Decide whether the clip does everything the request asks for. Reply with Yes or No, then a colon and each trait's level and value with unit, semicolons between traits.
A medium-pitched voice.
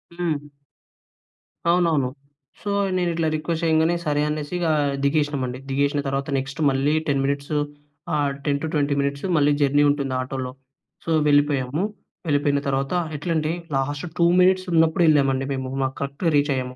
Yes: medium, 145 Hz